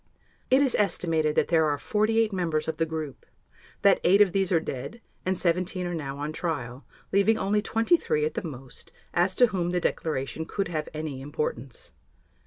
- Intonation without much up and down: No, average, 4.5 semitones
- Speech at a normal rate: Yes, average, 185 wpm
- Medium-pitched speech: Yes, medium, 170 Hz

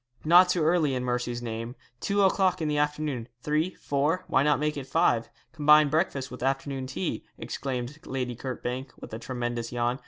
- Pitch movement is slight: No, average, 3.8 semitones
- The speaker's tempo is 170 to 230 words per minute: Yes, average, 180 wpm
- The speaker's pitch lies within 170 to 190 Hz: No, low, 135 Hz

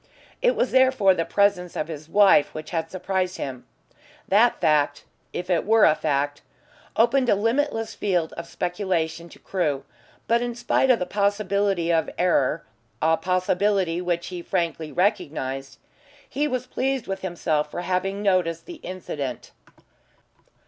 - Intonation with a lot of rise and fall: No, average, 4.3 semitones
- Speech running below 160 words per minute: Yes, average, 150 wpm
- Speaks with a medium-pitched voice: Yes, medium, 180 Hz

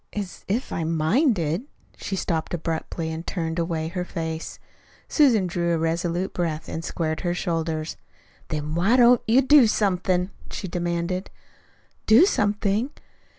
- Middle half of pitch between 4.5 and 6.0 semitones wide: No, average, 4.0 semitones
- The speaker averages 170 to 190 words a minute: No, average, 145 wpm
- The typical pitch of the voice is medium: Yes, medium, 175 Hz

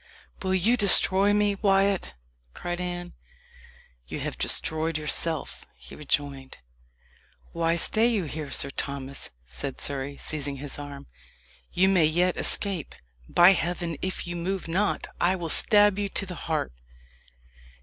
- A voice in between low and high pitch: Yes, medium, 175 Hz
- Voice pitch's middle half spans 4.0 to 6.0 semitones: Yes, average, 4.8 semitones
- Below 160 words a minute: Yes, average, 140 wpm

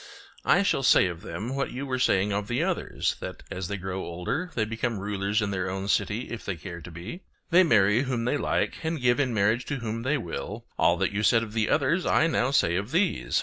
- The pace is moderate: No, fast, 240 wpm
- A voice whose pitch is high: No, low, 115 Hz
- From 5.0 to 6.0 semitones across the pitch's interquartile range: Yes, average, 5.3 semitones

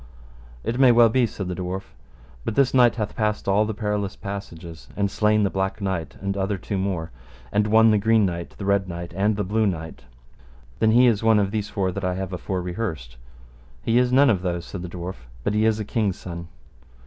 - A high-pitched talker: No, low, 100 Hz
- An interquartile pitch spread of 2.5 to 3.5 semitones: Yes, average, 3.1 semitones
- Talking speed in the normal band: No, fast, 220 wpm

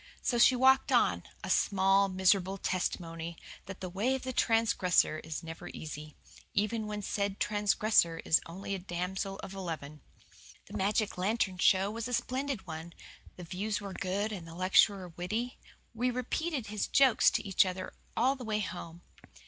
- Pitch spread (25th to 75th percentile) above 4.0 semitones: No, average, 3.6 semitones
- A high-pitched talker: Yes, high, 195 Hz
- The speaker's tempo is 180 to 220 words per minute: No, average, 165 wpm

